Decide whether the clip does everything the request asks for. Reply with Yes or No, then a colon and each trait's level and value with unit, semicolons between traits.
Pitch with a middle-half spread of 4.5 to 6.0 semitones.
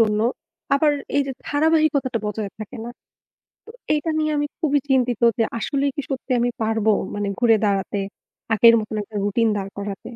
Yes: average, 5.1 semitones